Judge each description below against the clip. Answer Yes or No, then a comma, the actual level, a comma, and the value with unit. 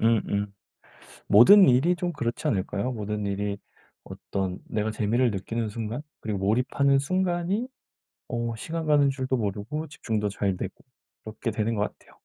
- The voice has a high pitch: No, low, 115 Hz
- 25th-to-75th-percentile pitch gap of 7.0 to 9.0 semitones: No, average, 5.2 semitones